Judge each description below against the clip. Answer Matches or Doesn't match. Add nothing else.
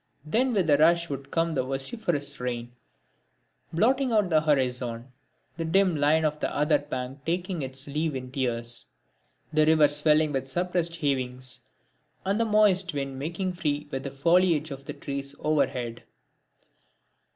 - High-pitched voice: Doesn't match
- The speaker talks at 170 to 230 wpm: Doesn't match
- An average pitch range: Matches